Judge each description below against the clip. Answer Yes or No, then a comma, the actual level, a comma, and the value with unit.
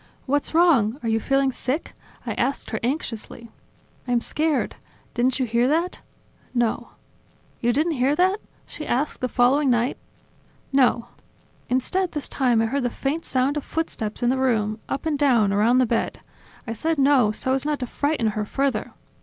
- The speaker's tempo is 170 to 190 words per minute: Yes, average, 175 wpm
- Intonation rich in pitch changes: No, average, 3.6 semitones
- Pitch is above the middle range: Yes, very high, 260 Hz